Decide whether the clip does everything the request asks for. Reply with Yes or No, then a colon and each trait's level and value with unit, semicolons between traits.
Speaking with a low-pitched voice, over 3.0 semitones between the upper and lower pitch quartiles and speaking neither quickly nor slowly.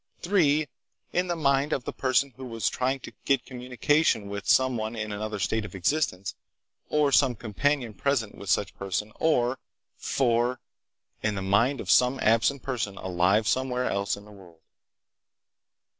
Yes: low, 120 Hz; average, 4.9 semitones; average, 160 wpm